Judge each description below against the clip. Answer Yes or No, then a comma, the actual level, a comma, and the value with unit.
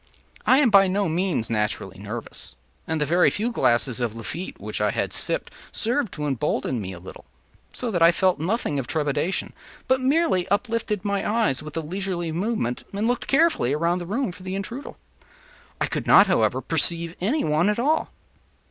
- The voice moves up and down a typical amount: No, wide, 6.7 semitones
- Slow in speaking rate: No, average, 185 wpm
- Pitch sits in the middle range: Yes, medium, 180 Hz